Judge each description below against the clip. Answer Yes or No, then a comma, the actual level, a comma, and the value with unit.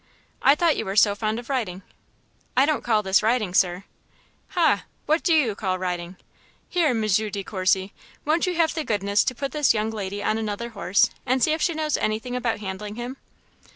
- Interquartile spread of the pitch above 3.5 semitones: Yes, wide, 5.6 semitones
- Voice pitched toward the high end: Yes, high, 220 Hz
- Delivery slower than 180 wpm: No, average, 200 wpm